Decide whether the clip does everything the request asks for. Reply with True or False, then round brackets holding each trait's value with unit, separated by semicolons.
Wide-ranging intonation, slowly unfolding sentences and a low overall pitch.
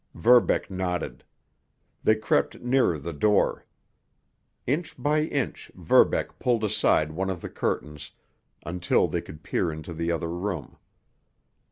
True (5.8 semitones; 130 wpm; 90 Hz)